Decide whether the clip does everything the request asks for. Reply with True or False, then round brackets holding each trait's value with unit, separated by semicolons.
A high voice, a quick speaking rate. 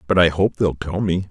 False (90 Hz; 275 wpm)